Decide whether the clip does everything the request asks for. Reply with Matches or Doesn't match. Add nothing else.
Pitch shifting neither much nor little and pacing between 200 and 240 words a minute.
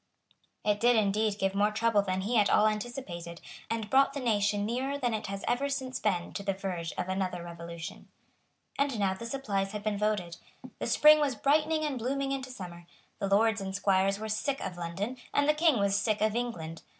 Matches